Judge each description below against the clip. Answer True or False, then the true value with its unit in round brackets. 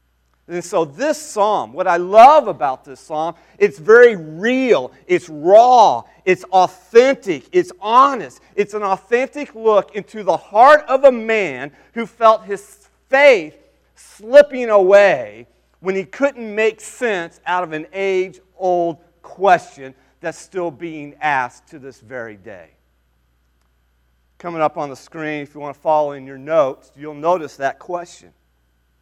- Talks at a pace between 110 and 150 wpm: True (145 wpm)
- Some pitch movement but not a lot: False (7.7 semitones)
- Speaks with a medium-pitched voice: True (175 Hz)